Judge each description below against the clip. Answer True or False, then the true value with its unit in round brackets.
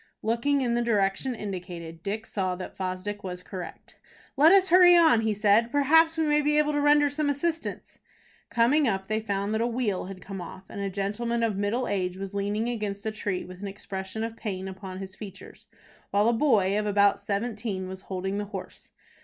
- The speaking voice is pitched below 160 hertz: False (210 Hz)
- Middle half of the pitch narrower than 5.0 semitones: True (3.9 semitones)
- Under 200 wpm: False (205 wpm)